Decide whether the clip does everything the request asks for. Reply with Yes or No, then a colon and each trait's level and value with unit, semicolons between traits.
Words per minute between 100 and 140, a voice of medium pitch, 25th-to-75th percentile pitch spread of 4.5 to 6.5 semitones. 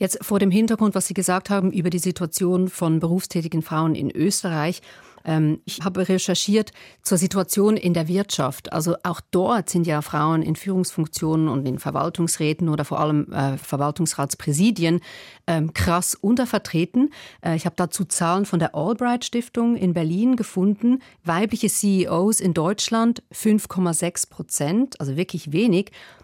No: average, 135 wpm; medium, 180 Hz; average, 3.6 semitones